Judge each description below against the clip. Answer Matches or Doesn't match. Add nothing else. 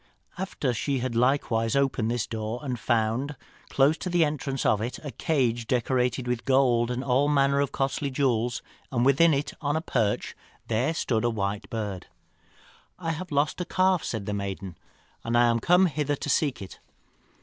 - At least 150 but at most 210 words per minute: Matches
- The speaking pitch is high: Doesn't match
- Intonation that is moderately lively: Matches